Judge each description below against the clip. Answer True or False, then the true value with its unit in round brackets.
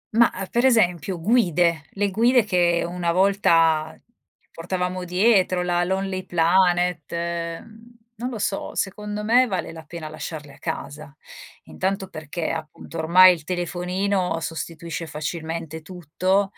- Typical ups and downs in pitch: True (3.0 semitones)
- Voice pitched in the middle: True (180 Hz)